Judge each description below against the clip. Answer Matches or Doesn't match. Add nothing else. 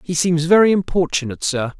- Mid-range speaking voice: Matches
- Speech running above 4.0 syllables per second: Matches